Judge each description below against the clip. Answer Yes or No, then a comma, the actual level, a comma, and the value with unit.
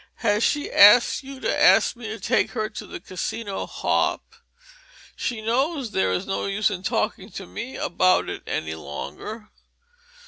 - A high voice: Yes, high, 215 Hz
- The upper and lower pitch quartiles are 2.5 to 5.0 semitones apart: Yes, average, 3.8 semitones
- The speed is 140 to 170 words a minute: Yes, average, 165 wpm